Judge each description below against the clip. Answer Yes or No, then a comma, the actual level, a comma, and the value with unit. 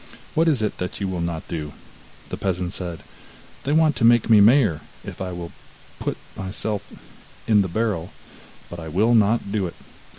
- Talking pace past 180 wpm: Yes, average, 190 wpm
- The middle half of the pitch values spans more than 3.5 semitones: Yes, average, 4.5 semitones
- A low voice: Yes, low, 100 Hz